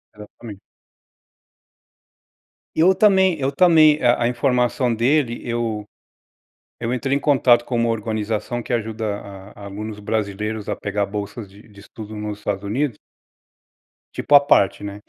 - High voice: No, low, 115 Hz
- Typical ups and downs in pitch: Yes, average, 3.5 semitones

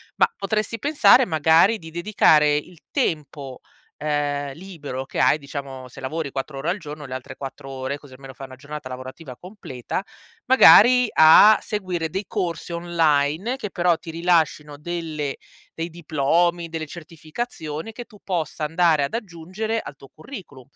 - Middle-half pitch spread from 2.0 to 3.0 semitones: No, average, 4.2 semitones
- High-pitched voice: No, medium, 160 Hz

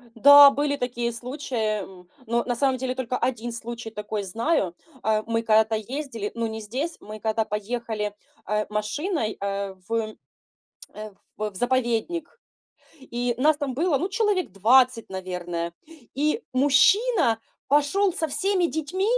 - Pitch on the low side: No, high, 240 Hz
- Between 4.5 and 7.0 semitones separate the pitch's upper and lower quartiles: Yes, average, 5.0 semitones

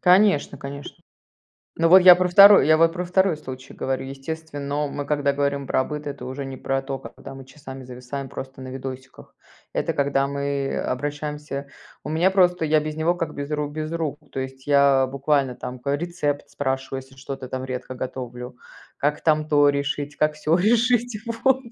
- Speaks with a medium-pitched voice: Yes, medium, 145 Hz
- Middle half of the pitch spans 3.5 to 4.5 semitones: No, average, 2.8 semitones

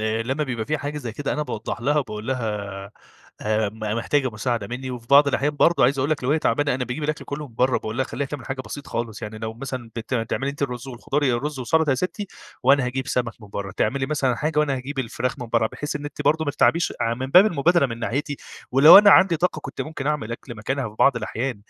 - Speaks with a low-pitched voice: Yes, low, 130 Hz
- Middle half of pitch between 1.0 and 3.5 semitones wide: No, average, 3.9 semitones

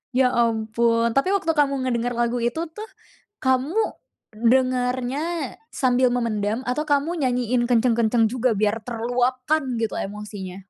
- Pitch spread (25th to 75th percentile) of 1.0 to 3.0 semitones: Yes, narrow, 2.4 semitones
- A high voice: Yes, high, 245 Hz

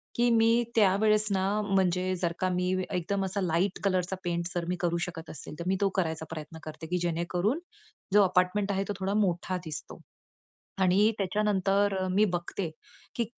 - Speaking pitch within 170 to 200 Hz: Yes, medium, 185 Hz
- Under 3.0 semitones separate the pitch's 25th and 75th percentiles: Yes, narrow, 2.6 semitones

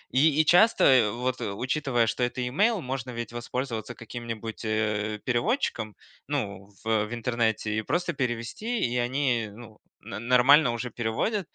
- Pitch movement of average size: Yes, average, 3.3 semitones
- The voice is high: No, low, 120 Hz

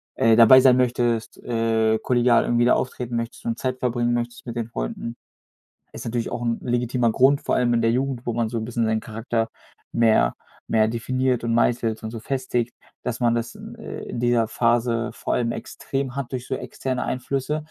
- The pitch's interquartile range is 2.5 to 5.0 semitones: No, narrow, 1.5 semitones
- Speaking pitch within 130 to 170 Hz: No, low, 120 Hz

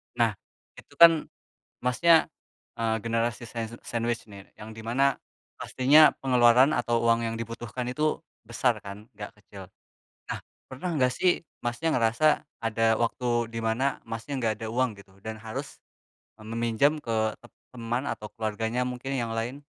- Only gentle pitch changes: Yes, narrow, 2.2 semitones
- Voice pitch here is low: Yes, low, 115 Hz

